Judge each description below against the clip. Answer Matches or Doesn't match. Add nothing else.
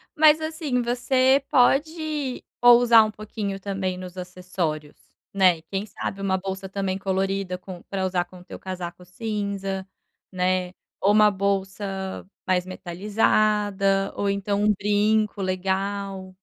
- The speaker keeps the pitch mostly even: Matches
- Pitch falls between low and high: Doesn't match